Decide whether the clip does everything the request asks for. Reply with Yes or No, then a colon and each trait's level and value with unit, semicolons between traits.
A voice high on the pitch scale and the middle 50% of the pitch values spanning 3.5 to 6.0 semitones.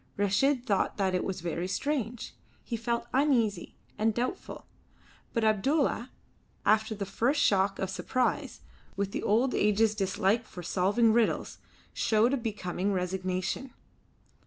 Yes: high, 215 Hz; average, 3.9 semitones